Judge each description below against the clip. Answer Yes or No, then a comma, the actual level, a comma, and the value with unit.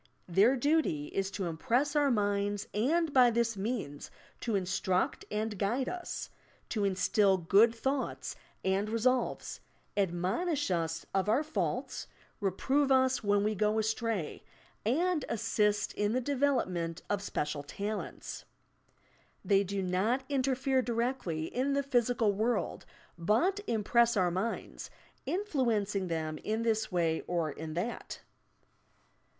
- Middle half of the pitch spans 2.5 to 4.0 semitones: No, average, 5.0 semitones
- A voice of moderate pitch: No, high, 215 Hz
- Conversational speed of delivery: No, slow, 130 wpm